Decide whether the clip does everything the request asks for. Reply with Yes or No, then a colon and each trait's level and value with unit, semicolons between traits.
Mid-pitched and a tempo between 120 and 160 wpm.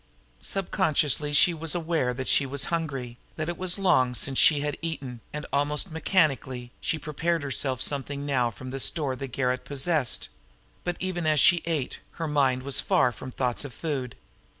No: medium, 145 Hz; average, 175 wpm